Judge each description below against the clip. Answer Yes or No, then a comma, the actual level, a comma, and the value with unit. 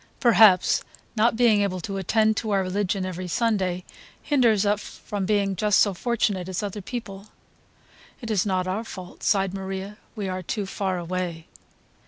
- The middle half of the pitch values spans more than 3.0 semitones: No, narrow, 2.5 semitones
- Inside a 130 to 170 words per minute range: Yes, average, 165 wpm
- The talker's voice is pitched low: No, high, 195 Hz